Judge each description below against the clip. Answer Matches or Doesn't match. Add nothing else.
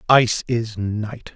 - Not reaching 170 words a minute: Matches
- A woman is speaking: Doesn't match